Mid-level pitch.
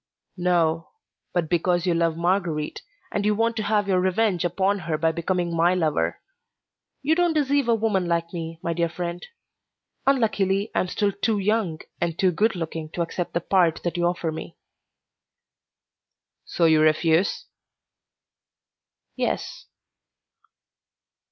Yes: medium, 175 Hz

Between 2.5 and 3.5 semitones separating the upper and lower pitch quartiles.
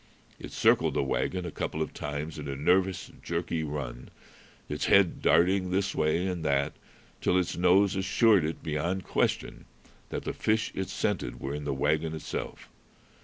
No: average, 4.0 semitones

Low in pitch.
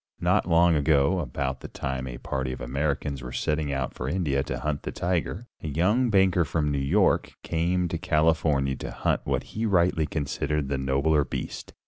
Yes: very low, 75 Hz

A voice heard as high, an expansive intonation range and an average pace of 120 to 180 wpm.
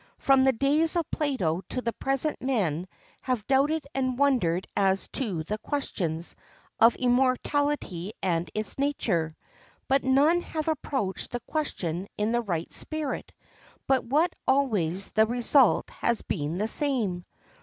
Yes: high, 245 Hz; wide, 6.7 semitones; average, 140 wpm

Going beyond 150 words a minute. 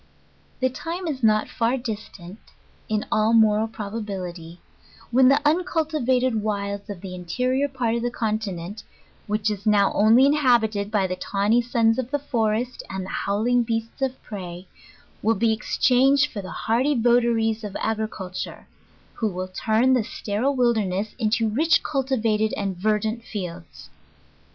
No: average, 145 wpm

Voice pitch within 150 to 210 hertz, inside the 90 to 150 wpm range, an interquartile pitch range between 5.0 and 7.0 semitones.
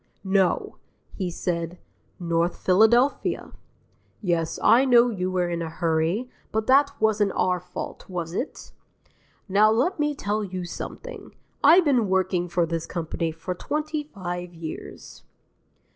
Yes: medium, 185 Hz; slow, 135 wpm; wide, 5.6 semitones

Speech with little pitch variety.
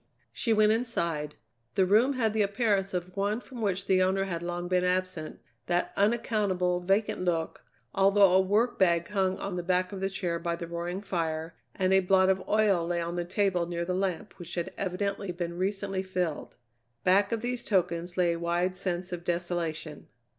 Yes: narrow, 2.3 semitones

